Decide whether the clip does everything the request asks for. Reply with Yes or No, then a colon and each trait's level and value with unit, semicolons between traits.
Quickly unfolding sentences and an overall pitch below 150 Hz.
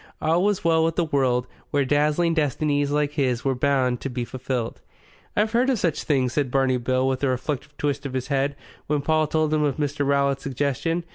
Yes: fast, 215 wpm; medium, 140 Hz